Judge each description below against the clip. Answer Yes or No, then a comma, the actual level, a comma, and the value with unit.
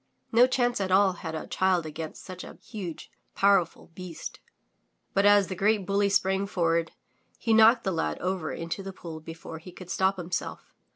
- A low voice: No, medium, 185 Hz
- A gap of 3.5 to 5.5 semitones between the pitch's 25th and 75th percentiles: No, average, 3.1 semitones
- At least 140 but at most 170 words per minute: No, average, 180 wpm